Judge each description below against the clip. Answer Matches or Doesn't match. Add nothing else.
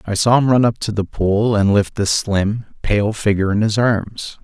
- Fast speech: Matches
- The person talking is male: Matches